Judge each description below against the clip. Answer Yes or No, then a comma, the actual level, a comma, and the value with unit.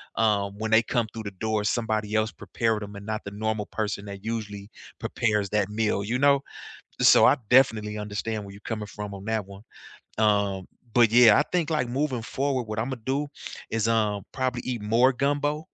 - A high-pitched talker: No, low, 110 Hz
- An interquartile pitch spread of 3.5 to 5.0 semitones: No, average, 2.7 semitones